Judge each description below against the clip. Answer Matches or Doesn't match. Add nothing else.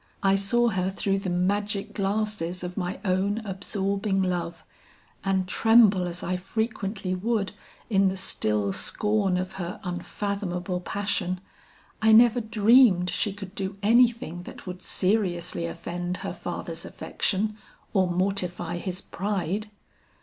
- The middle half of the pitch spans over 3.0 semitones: Doesn't match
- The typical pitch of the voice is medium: Doesn't match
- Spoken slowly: Matches